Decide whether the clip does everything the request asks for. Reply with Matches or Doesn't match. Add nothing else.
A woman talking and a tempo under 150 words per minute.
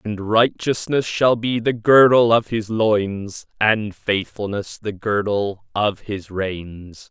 Doesn't match